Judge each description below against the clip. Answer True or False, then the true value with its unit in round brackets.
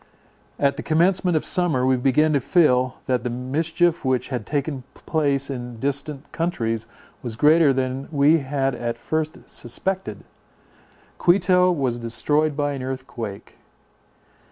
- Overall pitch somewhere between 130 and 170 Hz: True (140 Hz)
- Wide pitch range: False (3.8 semitones)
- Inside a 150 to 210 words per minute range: False (135 wpm)